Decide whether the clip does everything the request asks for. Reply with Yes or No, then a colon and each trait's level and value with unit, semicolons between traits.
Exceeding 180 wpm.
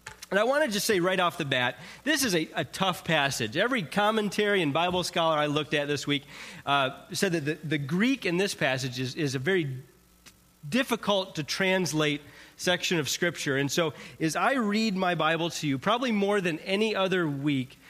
Yes: average, 200 wpm